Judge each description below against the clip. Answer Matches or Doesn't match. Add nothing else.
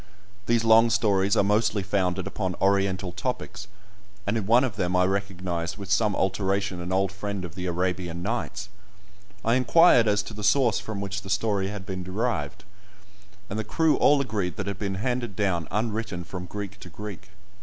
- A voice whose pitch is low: Matches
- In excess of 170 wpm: Matches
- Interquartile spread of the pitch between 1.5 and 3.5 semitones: Matches